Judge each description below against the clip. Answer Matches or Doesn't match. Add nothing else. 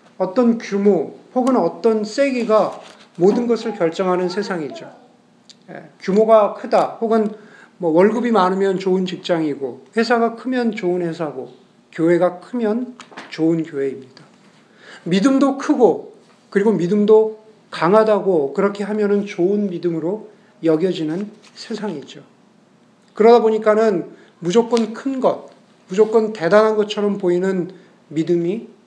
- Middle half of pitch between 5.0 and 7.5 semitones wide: Doesn't match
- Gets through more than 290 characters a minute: Doesn't match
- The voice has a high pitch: Matches